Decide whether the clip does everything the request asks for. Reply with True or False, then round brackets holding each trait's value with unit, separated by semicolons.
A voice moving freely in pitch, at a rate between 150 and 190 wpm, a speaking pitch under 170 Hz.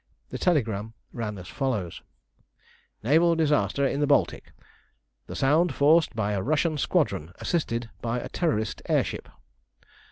False (6.0 semitones; 135 wpm; 135 Hz)